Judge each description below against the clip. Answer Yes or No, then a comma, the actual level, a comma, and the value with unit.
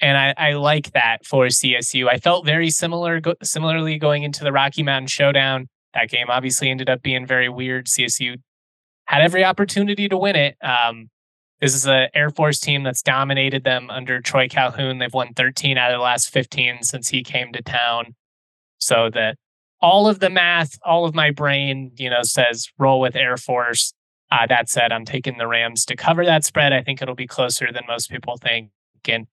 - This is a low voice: Yes, low, 130 Hz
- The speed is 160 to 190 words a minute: No, average, 200 wpm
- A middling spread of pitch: Yes, average, 3.1 semitones